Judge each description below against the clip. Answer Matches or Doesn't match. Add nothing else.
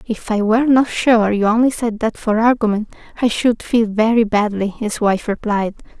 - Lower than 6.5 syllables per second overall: Matches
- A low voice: Doesn't match